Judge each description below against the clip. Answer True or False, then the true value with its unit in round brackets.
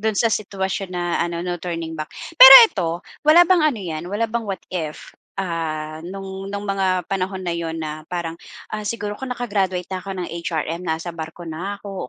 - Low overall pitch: False (185 Hz)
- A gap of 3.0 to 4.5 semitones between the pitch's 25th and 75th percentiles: True (3.3 semitones)